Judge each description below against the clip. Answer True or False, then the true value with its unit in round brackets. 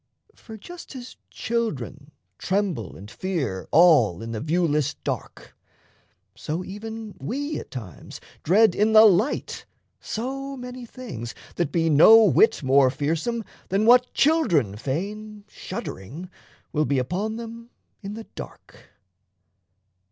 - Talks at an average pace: False (125 wpm)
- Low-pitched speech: False (195 Hz)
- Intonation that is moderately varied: False (7.8 semitones)